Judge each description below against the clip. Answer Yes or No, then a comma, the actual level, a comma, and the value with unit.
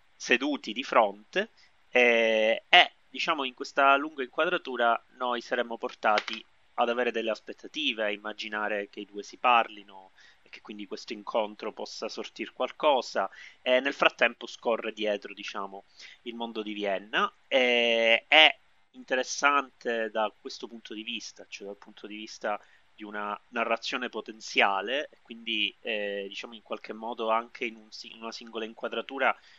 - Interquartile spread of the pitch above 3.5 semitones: No, average, 2.8 semitones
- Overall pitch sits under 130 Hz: Yes, low, 115 Hz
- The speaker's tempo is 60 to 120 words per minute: No, average, 150 wpm